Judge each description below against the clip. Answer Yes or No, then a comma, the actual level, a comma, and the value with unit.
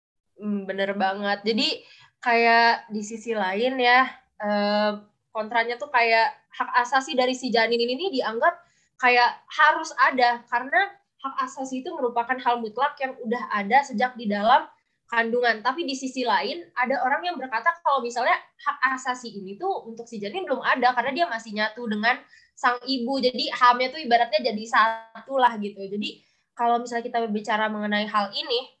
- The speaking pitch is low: No, high, 245 Hz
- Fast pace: Yes, fast, 160 wpm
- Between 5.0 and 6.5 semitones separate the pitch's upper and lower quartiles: No, average, 3.0 semitones